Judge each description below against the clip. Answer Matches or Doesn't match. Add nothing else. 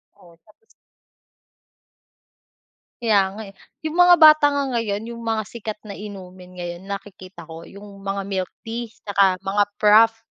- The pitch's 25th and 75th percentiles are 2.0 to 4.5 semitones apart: Matches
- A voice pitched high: Matches